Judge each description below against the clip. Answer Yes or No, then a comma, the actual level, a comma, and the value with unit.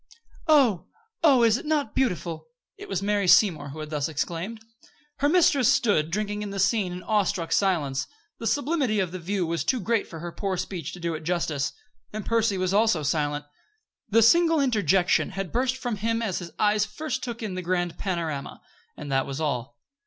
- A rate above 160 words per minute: Yes, average, 195 wpm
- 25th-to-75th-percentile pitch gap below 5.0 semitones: No, wide, 5.5 semitones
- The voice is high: Yes, high, 195 Hz